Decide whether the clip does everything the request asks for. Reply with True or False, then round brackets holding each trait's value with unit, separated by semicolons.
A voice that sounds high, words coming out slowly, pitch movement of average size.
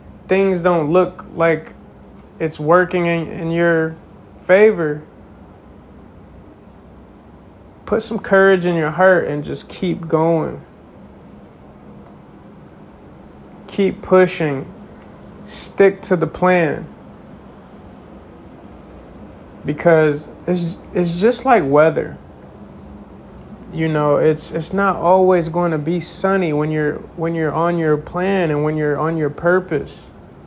False (165 Hz; 110 wpm; 3.3 semitones)